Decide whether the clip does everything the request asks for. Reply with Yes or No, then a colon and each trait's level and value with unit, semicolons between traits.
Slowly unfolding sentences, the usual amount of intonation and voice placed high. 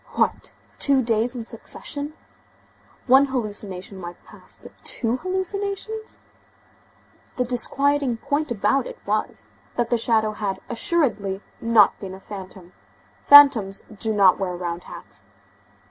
No: slow, 125 wpm; wide, 5.9 semitones; high, 230 Hz